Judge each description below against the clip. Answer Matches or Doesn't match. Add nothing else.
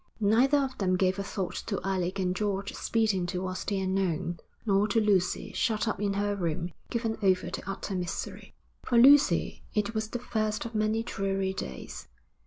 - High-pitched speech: Matches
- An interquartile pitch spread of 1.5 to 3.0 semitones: Matches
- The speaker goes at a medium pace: Matches